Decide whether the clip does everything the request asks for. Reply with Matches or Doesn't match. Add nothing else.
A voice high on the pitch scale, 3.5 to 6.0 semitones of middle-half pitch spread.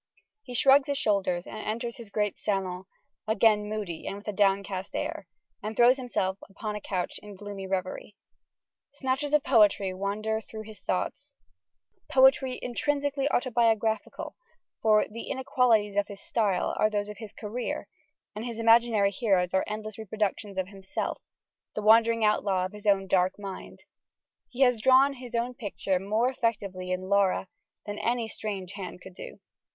Doesn't match